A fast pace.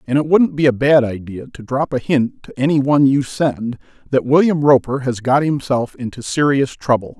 Yes: fast, 210 wpm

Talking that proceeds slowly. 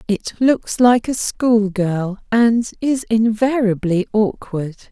Yes: slow, 120 wpm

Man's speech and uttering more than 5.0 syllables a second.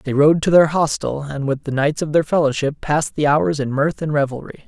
Yes: male; 5.5 syllables/s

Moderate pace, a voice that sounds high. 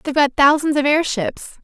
Yes: average, 185 wpm; very high, 290 Hz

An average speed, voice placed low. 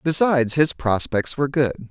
Yes: average, 155 wpm; low, 130 Hz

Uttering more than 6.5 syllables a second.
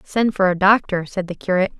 No: 6.1 syllables/s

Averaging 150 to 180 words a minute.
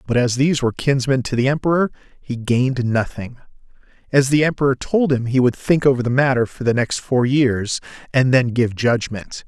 No: average, 195 wpm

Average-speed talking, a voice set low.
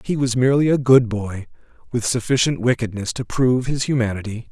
Yes: average, 175 wpm; low, 120 Hz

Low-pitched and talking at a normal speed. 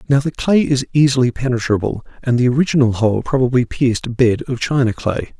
Yes: low, 125 Hz; average, 190 wpm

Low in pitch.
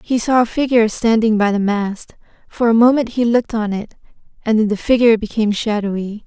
No: high, 220 Hz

